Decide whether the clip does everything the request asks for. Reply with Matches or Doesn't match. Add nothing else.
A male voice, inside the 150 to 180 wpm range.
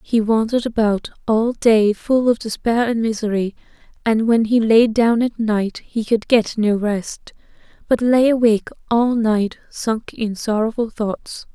Doesn't match